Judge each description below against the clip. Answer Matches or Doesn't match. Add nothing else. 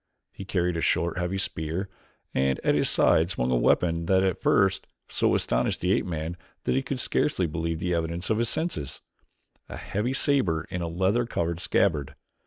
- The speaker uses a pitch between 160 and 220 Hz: Doesn't match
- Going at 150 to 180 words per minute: Doesn't match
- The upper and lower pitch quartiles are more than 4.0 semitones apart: Doesn't match